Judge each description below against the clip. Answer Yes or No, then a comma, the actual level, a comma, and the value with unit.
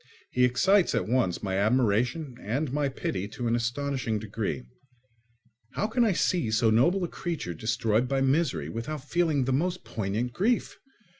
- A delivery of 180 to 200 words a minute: No, average, 160 wpm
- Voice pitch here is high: No, low, 125 Hz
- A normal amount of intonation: No, wide, 6.1 semitones